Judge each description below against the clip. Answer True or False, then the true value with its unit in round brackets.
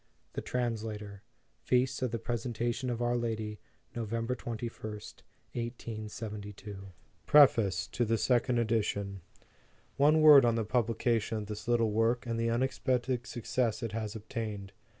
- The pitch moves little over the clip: True (2.1 semitones)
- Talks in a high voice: False (115 Hz)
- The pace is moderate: False (130 wpm)